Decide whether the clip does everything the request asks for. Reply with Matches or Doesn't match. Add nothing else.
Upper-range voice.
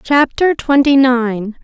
Matches